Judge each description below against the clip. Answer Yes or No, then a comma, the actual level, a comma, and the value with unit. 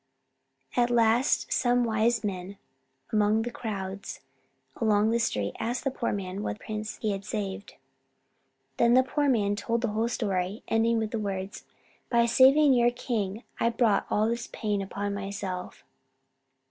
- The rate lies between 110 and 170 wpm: Yes, average, 155 wpm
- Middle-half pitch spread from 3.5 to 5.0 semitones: No, average, 2.8 semitones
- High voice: Yes, high, 220 Hz